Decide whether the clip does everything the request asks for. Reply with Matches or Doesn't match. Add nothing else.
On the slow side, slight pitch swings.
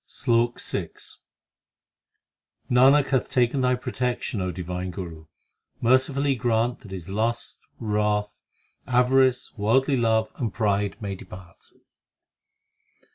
Doesn't match